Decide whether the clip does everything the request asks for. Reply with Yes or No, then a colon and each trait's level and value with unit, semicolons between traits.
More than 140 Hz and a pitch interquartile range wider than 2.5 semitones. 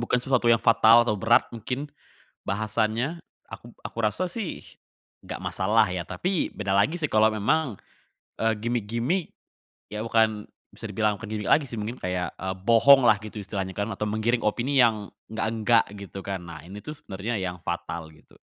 No: low, 110 Hz; average, 2.9 semitones